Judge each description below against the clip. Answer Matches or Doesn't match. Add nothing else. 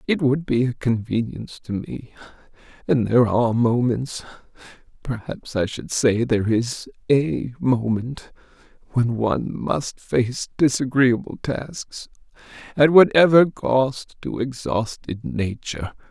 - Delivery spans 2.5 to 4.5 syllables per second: Matches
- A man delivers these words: Matches